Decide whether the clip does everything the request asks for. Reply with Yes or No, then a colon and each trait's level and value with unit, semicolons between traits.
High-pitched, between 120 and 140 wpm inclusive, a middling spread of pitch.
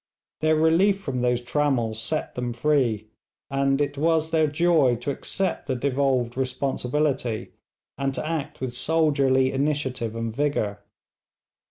No: low, 135 Hz; slow, 135 wpm; average, 3.7 semitones